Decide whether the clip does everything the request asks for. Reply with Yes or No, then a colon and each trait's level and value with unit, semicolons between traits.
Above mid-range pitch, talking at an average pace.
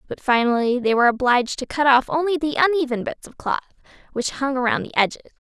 No: very high, 260 Hz; fast, 210 wpm